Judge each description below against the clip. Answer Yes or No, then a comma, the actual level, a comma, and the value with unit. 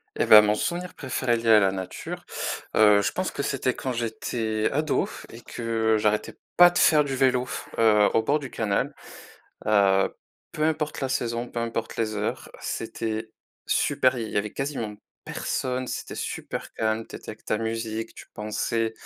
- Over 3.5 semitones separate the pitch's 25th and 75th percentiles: No, average, 3.1 semitones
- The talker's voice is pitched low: Yes, low, 115 Hz